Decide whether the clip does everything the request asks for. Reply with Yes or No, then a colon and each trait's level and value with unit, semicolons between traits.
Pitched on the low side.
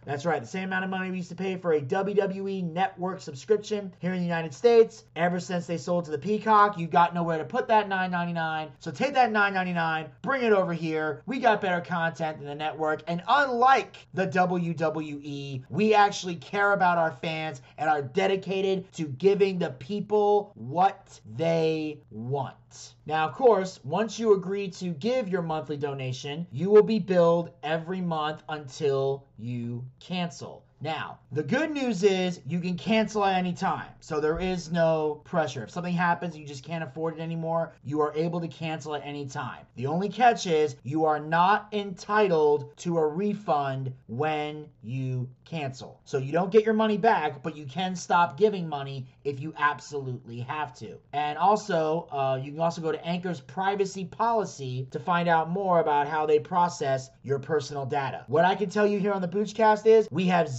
No: medium, 165 Hz